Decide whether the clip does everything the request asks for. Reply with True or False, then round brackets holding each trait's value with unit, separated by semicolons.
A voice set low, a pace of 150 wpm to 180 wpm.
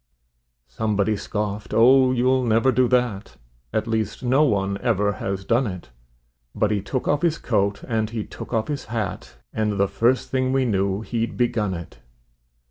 True (110 Hz; 170 wpm)